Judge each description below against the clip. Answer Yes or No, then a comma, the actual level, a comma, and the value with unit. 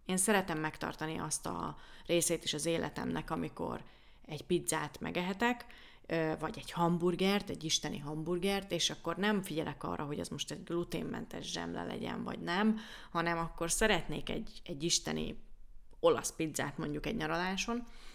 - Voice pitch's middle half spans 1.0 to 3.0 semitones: No, average, 3.6 semitones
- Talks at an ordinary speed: Yes, average, 145 wpm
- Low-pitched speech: No, medium, 170 Hz